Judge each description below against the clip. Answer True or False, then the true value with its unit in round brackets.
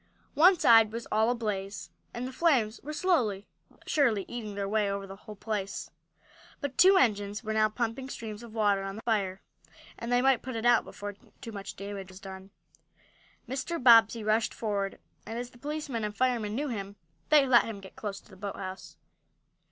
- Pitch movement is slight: False (3.4 semitones)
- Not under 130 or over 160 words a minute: False (190 wpm)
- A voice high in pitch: True (220 Hz)